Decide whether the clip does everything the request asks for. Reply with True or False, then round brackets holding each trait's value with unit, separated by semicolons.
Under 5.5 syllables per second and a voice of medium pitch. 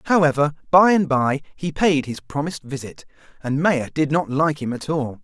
True (5.0 syllables/s; 150 Hz)